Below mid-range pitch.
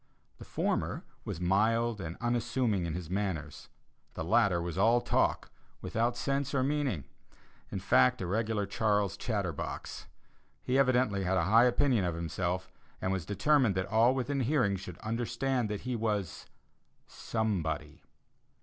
Yes: low, 105 Hz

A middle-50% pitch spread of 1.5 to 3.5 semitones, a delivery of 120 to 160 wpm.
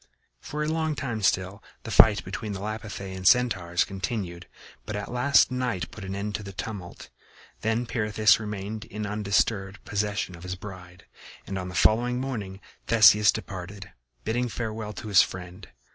No: average, 2.8 semitones; average, 170 wpm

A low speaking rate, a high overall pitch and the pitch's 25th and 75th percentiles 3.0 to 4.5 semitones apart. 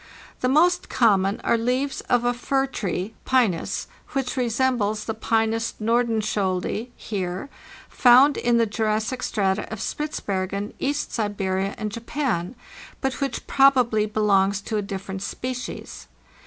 Yes: slow, 130 wpm; high, 225 Hz; average, 3.9 semitones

